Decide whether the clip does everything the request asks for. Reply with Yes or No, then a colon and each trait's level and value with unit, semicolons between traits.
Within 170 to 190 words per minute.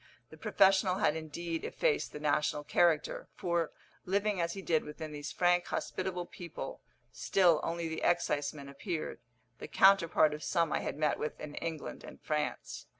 No: average, 160 wpm